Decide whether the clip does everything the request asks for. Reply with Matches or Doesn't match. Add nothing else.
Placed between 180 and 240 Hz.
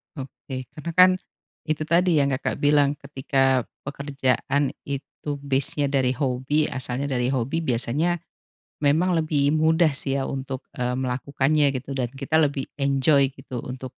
Doesn't match